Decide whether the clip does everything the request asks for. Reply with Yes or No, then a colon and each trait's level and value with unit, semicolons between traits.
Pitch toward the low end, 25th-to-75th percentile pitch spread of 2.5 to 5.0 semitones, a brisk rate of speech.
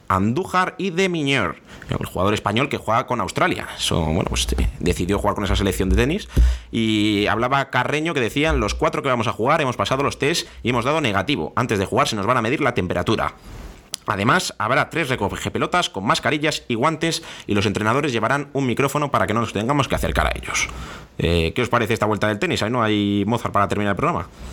No: low, 110 Hz; wide, 5.5 semitones; fast, 220 wpm